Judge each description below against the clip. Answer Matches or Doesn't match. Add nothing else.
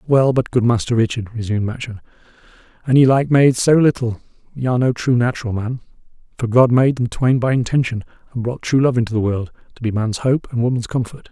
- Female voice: Doesn't match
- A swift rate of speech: Matches